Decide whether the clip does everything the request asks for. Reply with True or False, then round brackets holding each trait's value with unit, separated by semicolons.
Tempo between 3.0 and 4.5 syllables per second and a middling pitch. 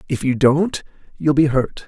True (4.3 syllables/s; 145 Hz)